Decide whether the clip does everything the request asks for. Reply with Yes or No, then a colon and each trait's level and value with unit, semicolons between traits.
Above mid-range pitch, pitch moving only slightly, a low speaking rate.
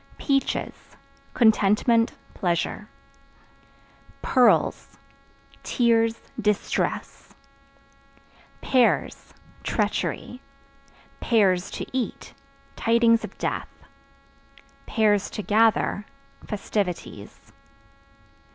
Yes: high, 225 Hz; narrow, 2.2 semitones; slow, 50 wpm